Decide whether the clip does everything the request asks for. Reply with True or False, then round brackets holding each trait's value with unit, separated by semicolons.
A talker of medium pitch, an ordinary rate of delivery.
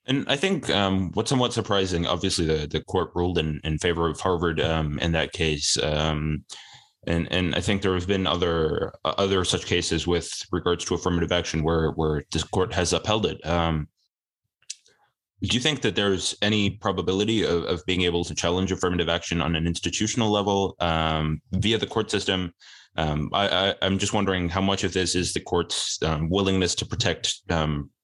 False (90 Hz; 190 wpm)